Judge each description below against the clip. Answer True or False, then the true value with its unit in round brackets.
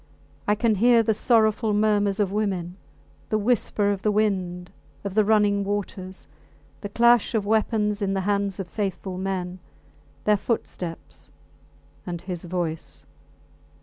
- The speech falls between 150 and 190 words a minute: False (140 wpm)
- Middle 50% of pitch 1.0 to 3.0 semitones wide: True (2.4 semitones)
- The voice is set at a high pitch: True (205 Hz)